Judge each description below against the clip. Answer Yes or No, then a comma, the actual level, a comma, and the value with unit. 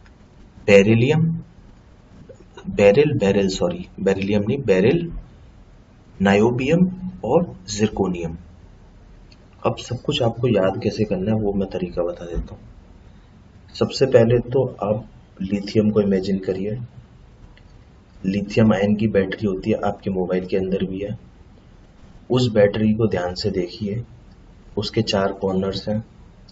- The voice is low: Yes, low, 100 Hz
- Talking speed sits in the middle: Yes, average, 120 wpm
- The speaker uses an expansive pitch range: No, average, 2.8 semitones